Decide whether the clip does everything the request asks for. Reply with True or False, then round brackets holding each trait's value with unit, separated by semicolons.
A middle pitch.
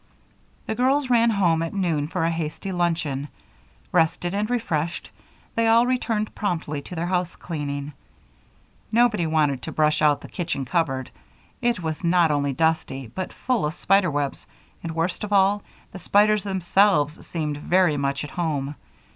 True (170 Hz)